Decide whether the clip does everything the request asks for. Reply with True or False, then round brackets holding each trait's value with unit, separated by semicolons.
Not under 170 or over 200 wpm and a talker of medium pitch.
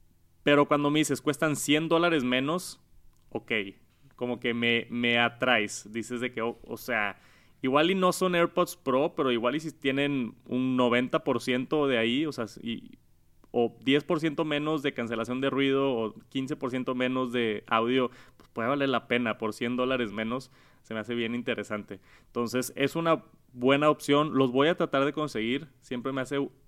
False (175 wpm; 130 Hz)